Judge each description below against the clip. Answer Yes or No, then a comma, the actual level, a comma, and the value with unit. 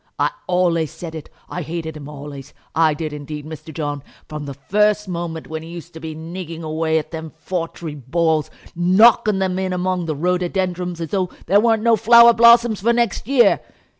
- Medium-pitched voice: Yes, medium, 170 Hz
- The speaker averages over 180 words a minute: Yes, average, 190 wpm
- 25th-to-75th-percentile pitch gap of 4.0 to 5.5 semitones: No, average, 3.2 semitones